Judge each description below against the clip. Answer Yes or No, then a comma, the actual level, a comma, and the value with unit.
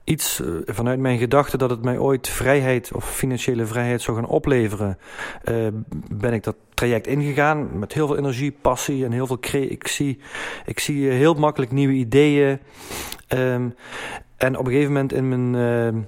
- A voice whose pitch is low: Yes, low, 130 Hz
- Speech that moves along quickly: No, average, 170 wpm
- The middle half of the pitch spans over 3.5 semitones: No, narrow, 2.5 semitones